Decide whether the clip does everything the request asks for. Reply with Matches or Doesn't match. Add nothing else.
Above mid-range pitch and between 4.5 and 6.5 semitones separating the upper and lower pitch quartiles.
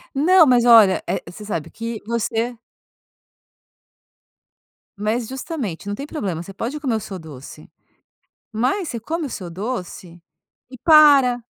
Matches